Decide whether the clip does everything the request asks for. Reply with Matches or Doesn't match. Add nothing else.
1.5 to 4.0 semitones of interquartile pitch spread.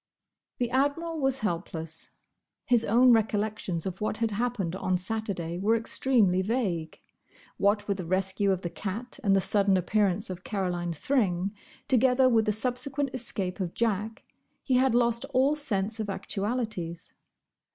Doesn't match